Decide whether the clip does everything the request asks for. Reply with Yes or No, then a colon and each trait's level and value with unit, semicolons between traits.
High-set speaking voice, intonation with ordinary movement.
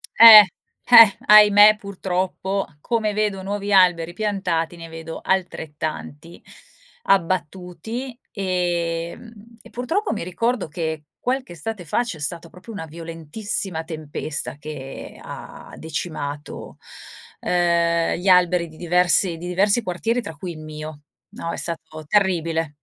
No: medium, 180 Hz; average, 3.8 semitones